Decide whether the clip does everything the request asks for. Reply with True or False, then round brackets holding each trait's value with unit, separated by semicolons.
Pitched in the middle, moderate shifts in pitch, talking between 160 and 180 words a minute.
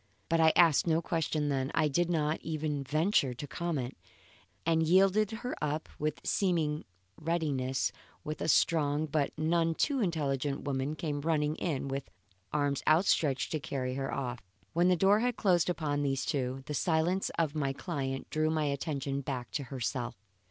True (150 Hz; 3.1 semitones; 165 wpm)